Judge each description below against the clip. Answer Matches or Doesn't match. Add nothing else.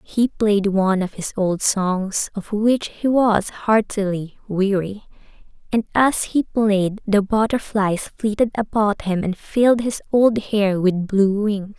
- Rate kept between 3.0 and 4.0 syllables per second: Matches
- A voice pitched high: Matches